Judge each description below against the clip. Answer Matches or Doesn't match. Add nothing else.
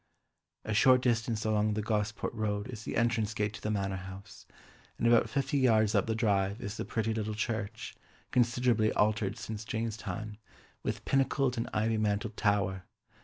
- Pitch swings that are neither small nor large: Doesn't match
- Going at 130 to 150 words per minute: Doesn't match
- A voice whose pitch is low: Matches